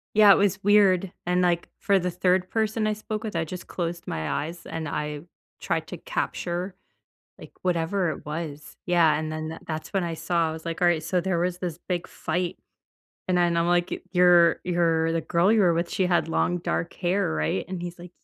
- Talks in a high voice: No, medium, 175 Hz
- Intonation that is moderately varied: No, narrow, 2.1 semitones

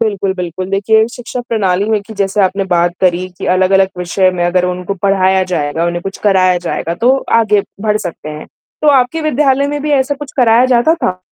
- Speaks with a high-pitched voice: Yes, high, 195 Hz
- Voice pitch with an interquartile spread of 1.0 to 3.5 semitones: No, average, 4.5 semitones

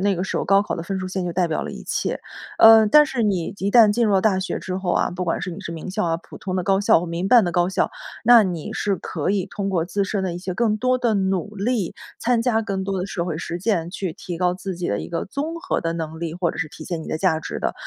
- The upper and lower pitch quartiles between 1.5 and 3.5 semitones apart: Yes, average, 3.1 semitones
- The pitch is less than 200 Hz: Yes, high, 190 Hz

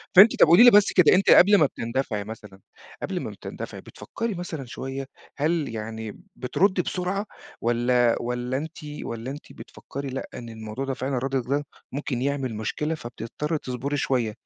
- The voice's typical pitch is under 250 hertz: Yes, low, 135 Hz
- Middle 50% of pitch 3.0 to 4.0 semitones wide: No, average, 5.0 semitones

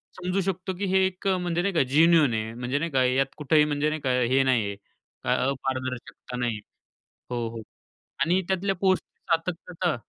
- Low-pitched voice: No, medium, 150 Hz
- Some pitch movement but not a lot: No, wide, 6.0 semitones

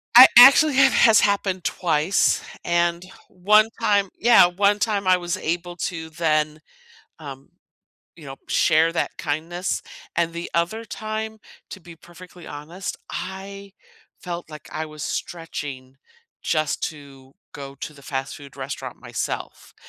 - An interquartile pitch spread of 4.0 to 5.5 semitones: Yes, average, 4.4 semitones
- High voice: No, medium, 170 Hz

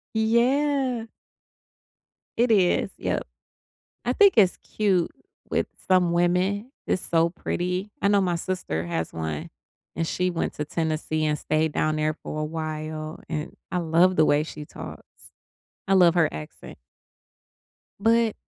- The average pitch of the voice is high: No, medium, 175 Hz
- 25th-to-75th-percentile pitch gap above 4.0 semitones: Yes, average, 4.5 semitones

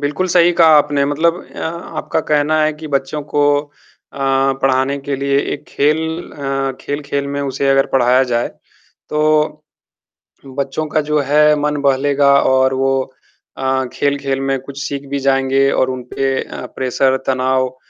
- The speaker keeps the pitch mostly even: Yes, narrow, 1.8 semitones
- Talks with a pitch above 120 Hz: Yes, medium, 140 Hz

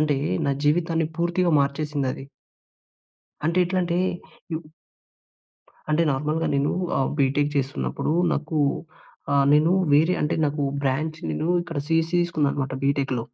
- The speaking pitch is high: No, medium, 150 Hz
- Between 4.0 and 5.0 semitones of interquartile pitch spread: No, average, 2.8 semitones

